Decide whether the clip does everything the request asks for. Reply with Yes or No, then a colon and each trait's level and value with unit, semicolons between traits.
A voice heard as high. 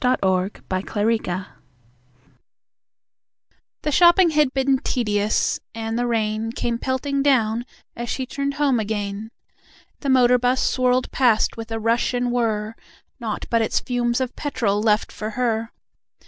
Yes: high, 235 Hz